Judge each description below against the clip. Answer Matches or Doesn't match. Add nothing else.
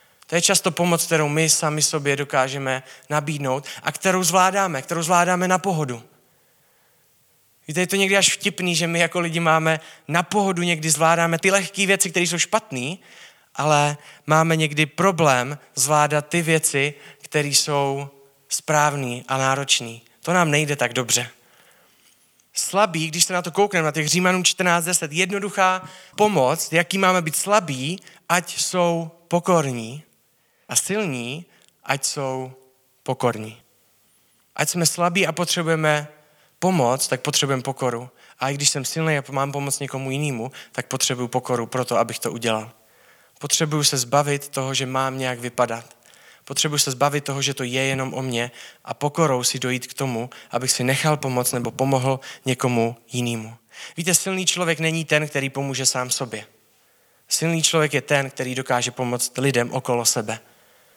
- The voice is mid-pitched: Matches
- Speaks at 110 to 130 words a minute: Doesn't match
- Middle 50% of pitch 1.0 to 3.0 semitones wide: Doesn't match